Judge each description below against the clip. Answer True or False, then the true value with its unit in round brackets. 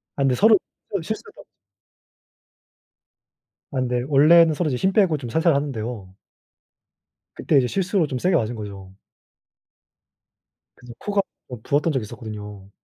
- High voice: False (140 Hz)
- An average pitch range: False (6.7 semitones)